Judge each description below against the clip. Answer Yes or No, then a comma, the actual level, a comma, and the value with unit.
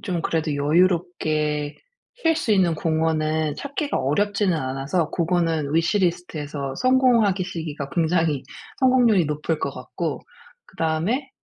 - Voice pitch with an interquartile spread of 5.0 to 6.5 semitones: No, average, 4.2 semitones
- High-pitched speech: No, medium, 165 Hz